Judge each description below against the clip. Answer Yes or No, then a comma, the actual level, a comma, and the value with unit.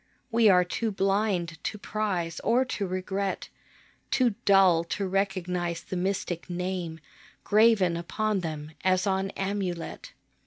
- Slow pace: Yes, slow, 125 wpm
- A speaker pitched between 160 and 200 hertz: Yes, high, 190 Hz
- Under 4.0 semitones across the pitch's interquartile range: Yes, narrow, 2.5 semitones